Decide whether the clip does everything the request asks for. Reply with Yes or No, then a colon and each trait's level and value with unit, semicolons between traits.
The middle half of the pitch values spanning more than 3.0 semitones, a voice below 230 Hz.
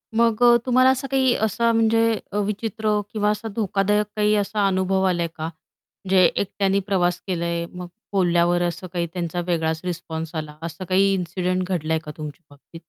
Yes: average, 3.7 semitones; medium, 185 Hz